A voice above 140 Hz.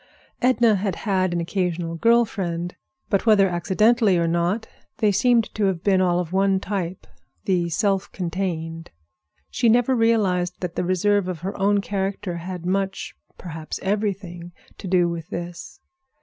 Yes: high, 190 Hz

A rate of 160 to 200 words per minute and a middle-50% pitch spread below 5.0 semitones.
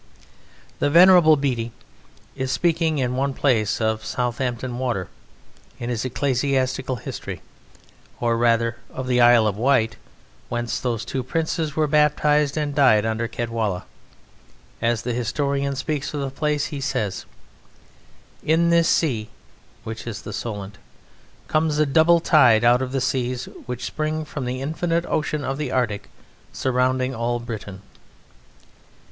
No: average, 140 wpm; average, 4.0 semitones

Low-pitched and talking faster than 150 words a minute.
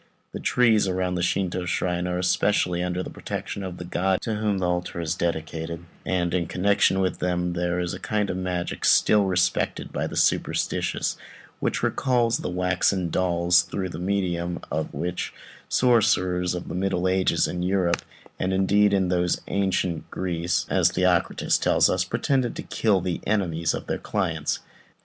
Yes: very low, 90 Hz; average, 170 wpm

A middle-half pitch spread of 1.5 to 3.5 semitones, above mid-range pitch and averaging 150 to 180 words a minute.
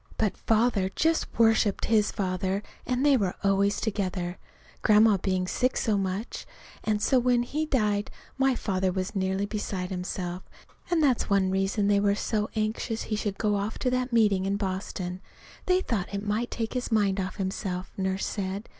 Yes: average, 2.9 semitones; high, 205 Hz; average, 170 wpm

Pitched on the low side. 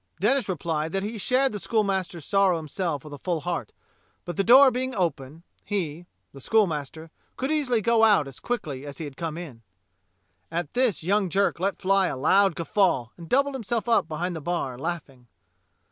No: medium, 180 Hz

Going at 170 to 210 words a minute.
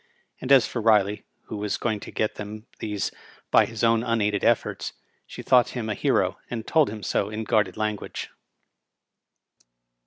Yes: average, 175 wpm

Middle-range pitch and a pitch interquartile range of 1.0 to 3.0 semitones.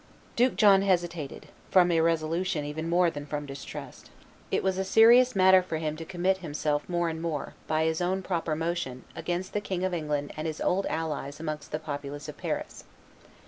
No: medium, 165 Hz; average, 3.4 semitones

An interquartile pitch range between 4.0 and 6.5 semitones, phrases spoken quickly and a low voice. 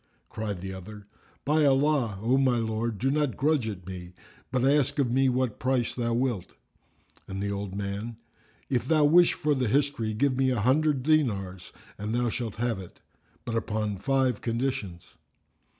No: average, 4.5 semitones; average, 170 wpm; low, 120 Hz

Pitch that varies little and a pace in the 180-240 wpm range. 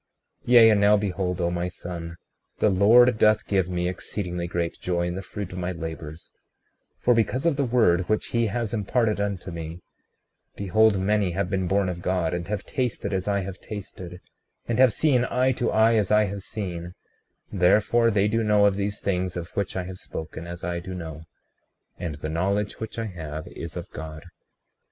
No: average, 3.4 semitones; average, 200 wpm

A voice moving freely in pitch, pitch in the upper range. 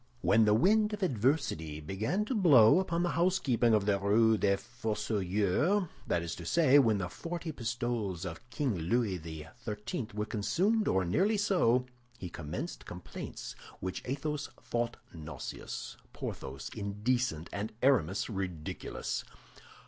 No: wide, 7.1 semitones; low, 115 Hz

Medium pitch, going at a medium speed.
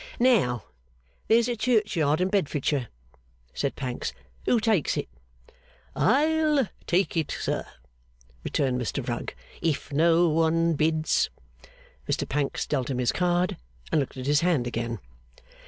No: medium, 160 Hz; slow, 130 wpm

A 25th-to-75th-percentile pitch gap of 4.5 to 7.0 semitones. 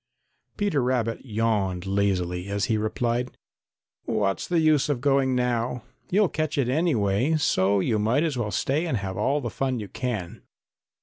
Yes: wide, 5.5 semitones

